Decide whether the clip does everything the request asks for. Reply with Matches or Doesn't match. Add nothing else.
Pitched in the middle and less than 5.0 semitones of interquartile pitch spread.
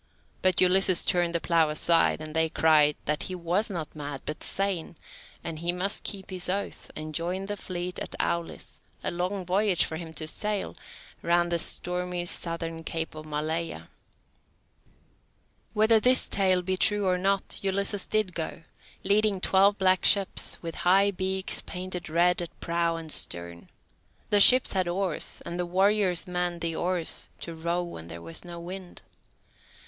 Matches